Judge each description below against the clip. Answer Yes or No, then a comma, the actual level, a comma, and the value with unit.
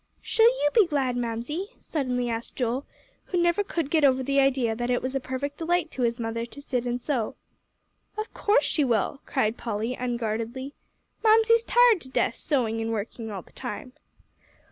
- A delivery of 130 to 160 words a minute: No, average, 185 wpm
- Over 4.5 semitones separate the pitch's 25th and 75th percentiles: Yes, average, 4.9 semitones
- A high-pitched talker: Yes, very high, 260 Hz